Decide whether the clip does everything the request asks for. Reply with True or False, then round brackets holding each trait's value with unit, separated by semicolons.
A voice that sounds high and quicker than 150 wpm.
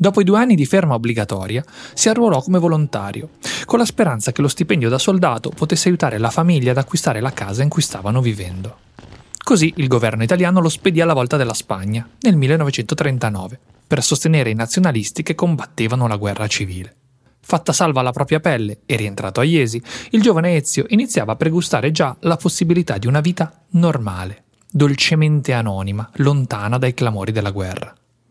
False (140 Hz; 170 wpm)